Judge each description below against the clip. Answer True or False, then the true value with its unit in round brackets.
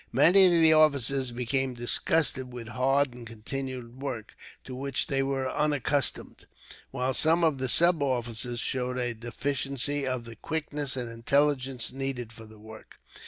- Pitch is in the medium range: False (130 Hz)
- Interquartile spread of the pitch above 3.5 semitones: False (2.8 semitones)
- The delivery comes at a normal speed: True (155 wpm)